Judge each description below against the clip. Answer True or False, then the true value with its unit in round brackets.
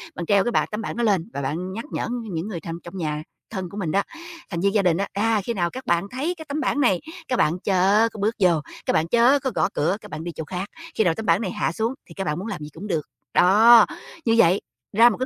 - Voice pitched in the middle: False (195 Hz)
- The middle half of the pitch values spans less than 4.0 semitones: False (4.7 semitones)